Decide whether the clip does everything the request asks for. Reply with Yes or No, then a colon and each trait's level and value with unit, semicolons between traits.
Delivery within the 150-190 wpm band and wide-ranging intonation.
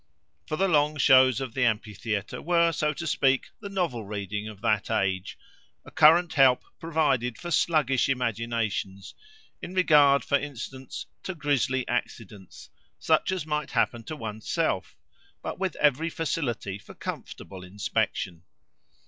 No: average, 140 wpm; wide, 6.1 semitones